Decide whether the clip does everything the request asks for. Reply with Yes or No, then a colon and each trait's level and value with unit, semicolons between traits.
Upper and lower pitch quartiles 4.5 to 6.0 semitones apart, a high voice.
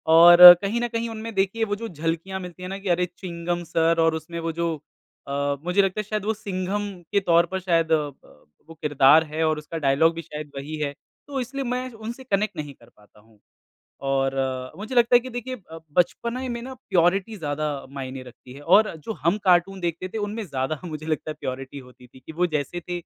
No: wide, 5.4 semitones; medium, 170 Hz